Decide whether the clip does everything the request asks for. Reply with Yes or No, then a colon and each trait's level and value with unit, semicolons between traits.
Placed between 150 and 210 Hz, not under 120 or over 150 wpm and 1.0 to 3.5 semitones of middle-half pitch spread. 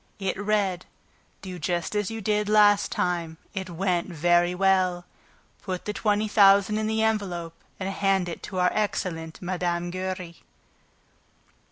Yes: medium, 185 Hz; average, 145 wpm; average, 2.7 semitones